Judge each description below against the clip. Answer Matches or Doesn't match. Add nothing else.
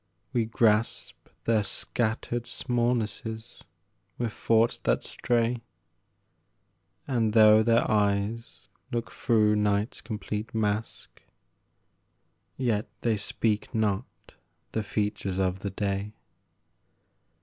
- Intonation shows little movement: Matches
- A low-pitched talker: Matches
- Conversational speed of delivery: Doesn't match